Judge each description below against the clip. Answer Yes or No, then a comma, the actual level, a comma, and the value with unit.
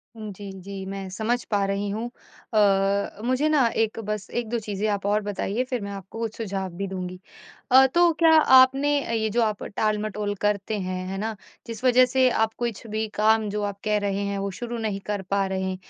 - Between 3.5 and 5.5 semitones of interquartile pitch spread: No, average, 2.7 semitones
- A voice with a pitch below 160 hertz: No, high, 210 Hz